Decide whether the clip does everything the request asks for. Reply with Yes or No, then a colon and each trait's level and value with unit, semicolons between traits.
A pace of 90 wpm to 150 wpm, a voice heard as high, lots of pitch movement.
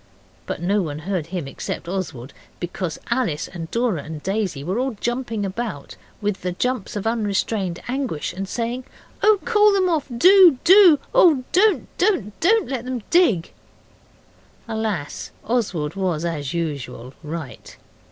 Yes: average, 145 wpm; high, 205 Hz; wide, 7.4 semitones